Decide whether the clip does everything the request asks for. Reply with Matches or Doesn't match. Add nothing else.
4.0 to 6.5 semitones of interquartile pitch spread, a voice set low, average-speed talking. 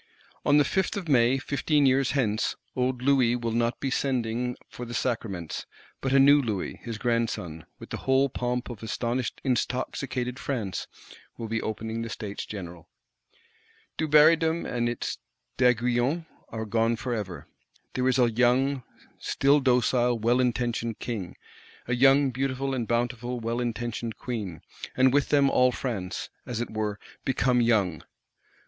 Doesn't match